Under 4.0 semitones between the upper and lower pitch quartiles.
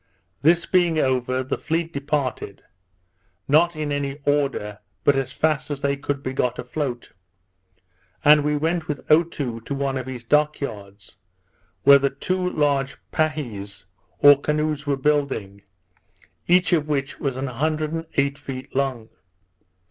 Yes: narrow, 2.6 semitones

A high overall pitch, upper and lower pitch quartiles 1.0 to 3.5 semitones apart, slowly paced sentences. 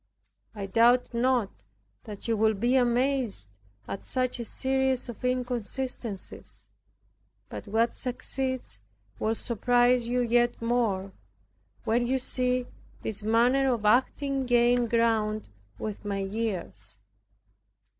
Yes: high, 240 Hz; narrow, 2.6 semitones; slow, 115 wpm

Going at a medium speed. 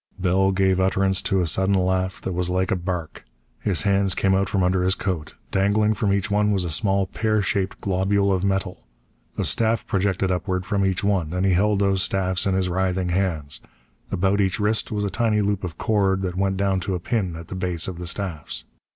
No: fast, 220 wpm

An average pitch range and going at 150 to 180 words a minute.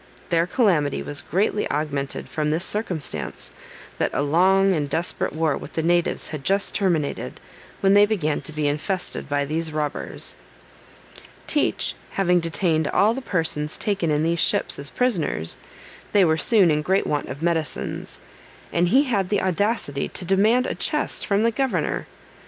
Yes: average, 4.6 semitones; average, 165 wpm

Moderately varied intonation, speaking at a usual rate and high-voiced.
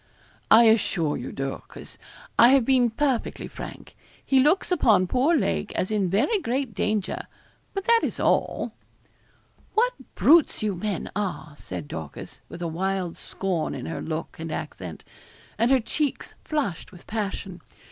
No: wide, 7.3 semitones; average, 150 wpm; high, 210 Hz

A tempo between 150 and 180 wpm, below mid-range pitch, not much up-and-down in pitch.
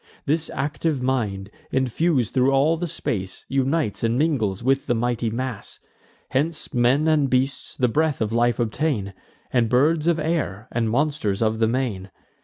No: average, 160 wpm; low, 130 Hz; average, 4.7 semitones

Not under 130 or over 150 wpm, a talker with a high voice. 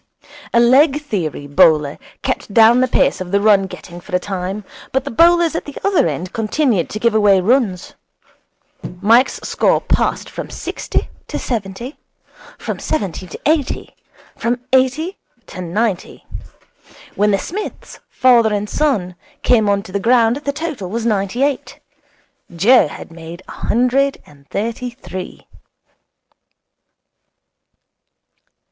Yes: average, 140 wpm; high, 220 Hz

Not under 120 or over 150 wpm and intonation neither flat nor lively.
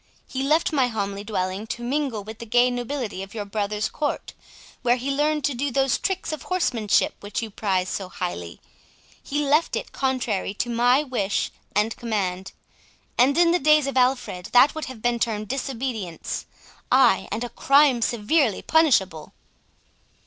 No: average, 165 wpm; average, 4.9 semitones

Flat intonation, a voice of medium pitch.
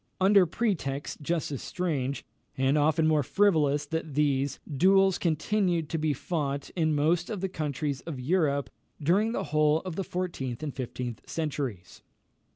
No: average, 4.0 semitones; medium, 155 Hz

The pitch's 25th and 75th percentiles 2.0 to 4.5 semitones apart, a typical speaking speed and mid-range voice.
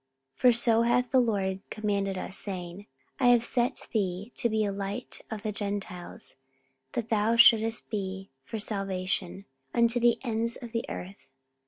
No: average, 3.1 semitones; average, 165 wpm; high, 215 Hz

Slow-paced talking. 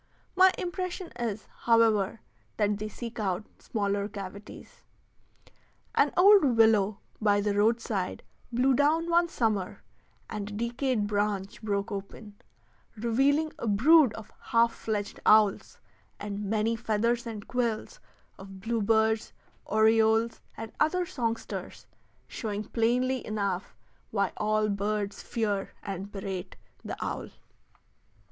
Yes: slow, 115 wpm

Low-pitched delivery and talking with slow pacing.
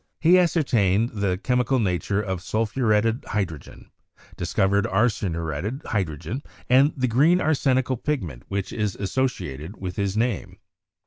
Yes: low, 105 Hz; slow, 130 wpm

